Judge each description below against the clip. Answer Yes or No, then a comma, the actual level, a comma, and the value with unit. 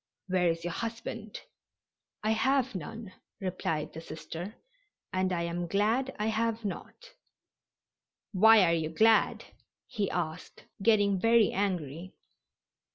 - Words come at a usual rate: No, slow, 120 wpm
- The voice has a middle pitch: No, high, 200 Hz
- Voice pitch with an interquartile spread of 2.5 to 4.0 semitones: No, average, 4.4 semitones